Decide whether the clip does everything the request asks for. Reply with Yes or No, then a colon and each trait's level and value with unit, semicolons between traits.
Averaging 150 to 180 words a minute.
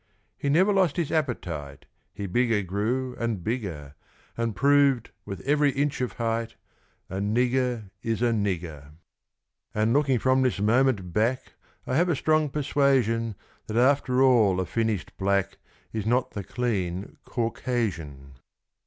No: average, 140 wpm